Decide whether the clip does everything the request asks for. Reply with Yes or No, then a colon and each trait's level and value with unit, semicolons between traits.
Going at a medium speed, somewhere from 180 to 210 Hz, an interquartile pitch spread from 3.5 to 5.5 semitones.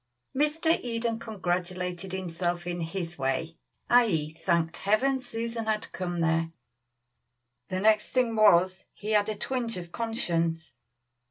No: slow, 125 wpm; high, 190 Hz; average, 4.9 semitones